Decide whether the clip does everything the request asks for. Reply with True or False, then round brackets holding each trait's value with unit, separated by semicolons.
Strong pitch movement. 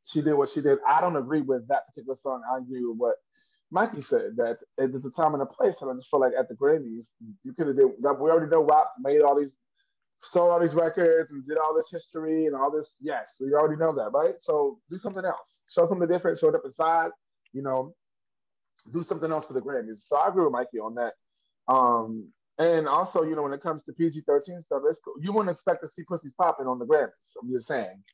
True (6.7 semitones)